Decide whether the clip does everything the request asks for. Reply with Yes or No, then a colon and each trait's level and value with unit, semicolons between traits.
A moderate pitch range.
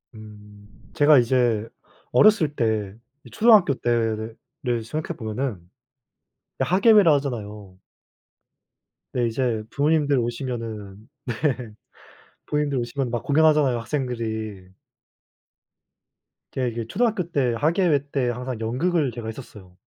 Yes: average, 4.9 semitones